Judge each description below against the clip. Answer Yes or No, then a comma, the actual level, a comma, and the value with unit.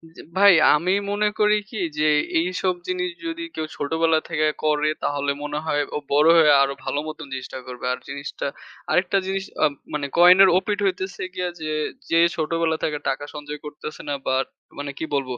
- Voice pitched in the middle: Yes, medium, 155 Hz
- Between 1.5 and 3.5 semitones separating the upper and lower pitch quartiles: No, average, 3.9 semitones